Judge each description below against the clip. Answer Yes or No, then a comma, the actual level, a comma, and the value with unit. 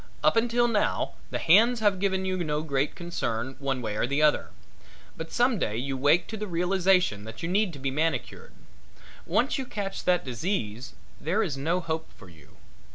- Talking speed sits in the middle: Yes, average, 190 wpm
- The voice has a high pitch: No, medium, 165 Hz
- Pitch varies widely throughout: Yes, wide, 6.3 semitones